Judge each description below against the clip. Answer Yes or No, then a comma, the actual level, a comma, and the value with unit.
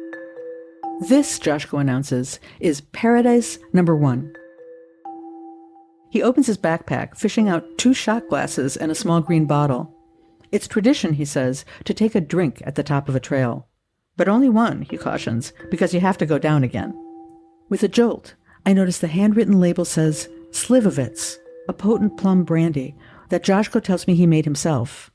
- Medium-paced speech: Yes, average, 160 wpm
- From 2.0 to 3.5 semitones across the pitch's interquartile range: No, average, 4.4 semitones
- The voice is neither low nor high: Yes, medium, 165 Hz